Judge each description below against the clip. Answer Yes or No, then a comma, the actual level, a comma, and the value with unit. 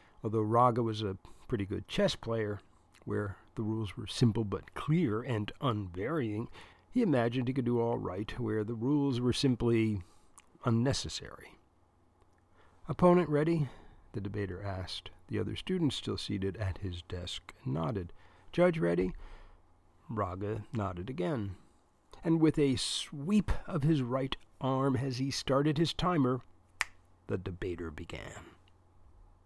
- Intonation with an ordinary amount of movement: No, wide, 6.2 semitones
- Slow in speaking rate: Yes, slow, 130 wpm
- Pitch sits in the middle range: No, low, 110 Hz